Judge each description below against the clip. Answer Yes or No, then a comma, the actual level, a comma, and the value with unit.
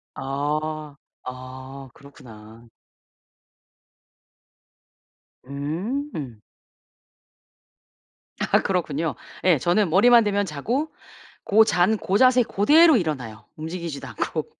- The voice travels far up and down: Yes, wide, 7.2 semitones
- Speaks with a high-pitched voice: No, medium, 155 Hz